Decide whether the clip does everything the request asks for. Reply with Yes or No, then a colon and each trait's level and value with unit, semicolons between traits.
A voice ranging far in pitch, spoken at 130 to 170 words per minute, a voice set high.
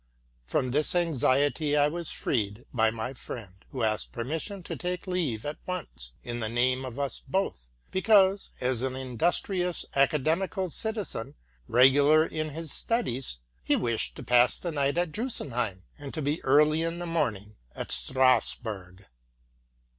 No: wide, 5.8 semitones; average, 150 wpm; medium, 140 Hz